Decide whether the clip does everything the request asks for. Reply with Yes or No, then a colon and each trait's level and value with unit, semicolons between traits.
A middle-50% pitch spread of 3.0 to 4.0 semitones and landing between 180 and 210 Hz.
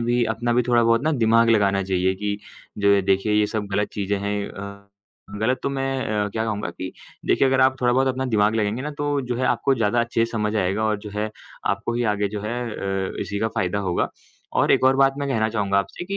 No: average, 3.3 semitones; low, 110 Hz